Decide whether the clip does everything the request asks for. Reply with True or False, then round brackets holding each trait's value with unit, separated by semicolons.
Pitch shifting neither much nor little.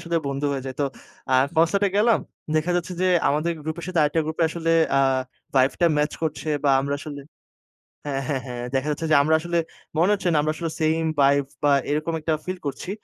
True (3.0 semitones)